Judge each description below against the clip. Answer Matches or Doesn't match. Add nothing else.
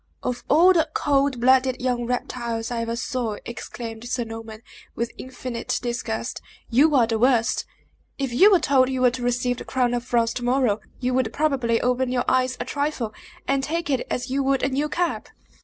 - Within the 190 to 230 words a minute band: Matches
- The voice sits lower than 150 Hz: Doesn't match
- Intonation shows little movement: Matches